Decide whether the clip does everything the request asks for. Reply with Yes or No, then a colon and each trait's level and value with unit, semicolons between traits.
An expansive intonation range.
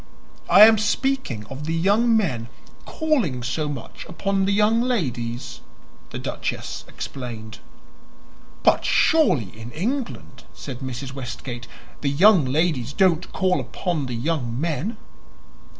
Yes: wide, 8.6 semitones